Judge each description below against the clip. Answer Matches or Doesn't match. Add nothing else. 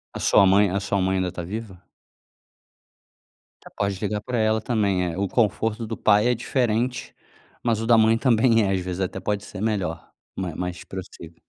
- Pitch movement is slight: Doesn't match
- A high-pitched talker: Doesn't match